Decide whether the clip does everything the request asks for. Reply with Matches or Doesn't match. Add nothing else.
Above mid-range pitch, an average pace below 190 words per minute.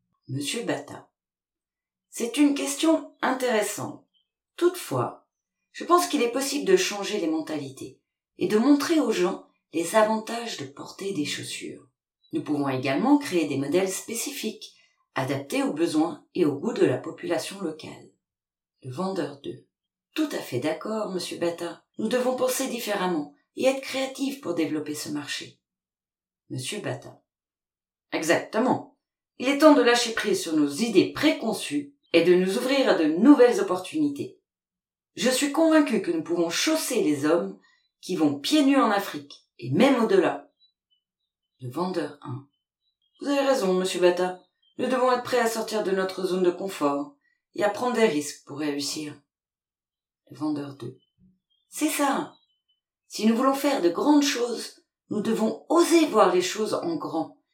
Matches